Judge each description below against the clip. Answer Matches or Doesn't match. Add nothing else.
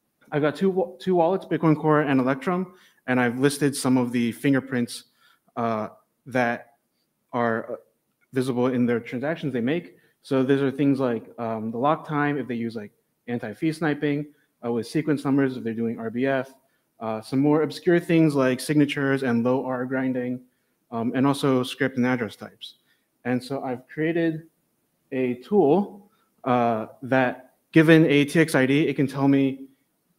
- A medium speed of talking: Matches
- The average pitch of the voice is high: Doesn't match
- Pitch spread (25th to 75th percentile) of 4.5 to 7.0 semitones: Doesn't match